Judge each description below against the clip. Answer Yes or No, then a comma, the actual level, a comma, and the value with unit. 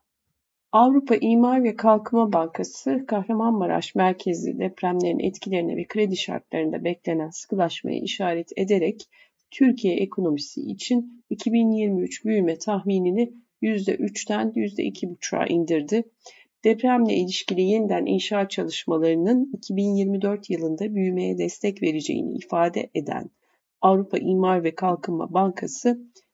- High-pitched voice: Yes, high, 195 Hz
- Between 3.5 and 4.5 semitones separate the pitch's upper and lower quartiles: Yes, average, 4.1 semitones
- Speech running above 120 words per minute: No, slow, 95 wpm